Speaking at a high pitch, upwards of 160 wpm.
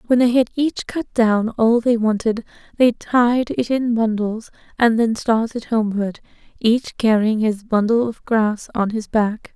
Yes: high, 225 Hz; average, 170 wpm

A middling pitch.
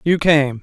Yes: medium, 150 Hz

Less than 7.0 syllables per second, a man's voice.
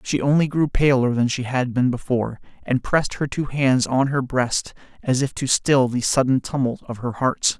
Yes: 4.9 syllables/s; male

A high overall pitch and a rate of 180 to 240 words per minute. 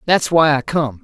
No: medium, 145 Hz; fast, 235 wpm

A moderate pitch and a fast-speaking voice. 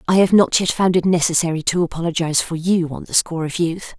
Yes: medium, 170 Hz; fast, 240 wpm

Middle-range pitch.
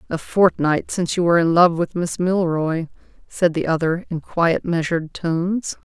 Yes: medium, 170 Hz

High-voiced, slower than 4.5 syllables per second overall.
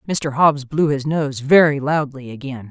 No: medium, 140 Hz; 4.3 syllables/s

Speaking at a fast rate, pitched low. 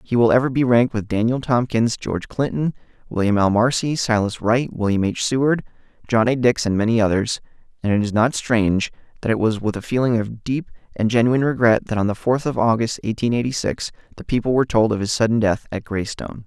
Yes: fast, 215 wpm; low, 115 Hz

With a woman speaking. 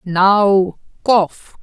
Yes: female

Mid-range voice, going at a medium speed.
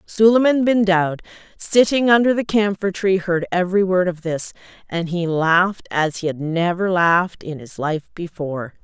Yes: medium, 180 Hz; average, 170 wpm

